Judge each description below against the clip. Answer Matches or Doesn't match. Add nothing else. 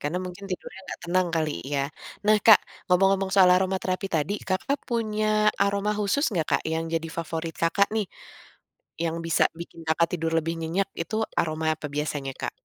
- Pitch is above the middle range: Doesn't match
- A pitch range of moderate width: Matches